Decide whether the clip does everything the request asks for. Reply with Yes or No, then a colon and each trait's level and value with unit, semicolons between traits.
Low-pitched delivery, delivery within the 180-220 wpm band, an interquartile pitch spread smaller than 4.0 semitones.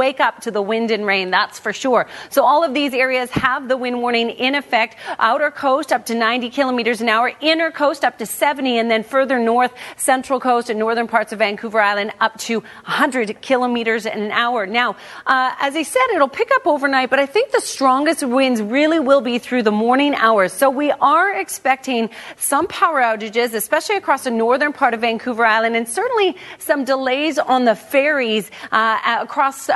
No: very high, 250 Hz; average, 200 wpm; average, 3.6 semitones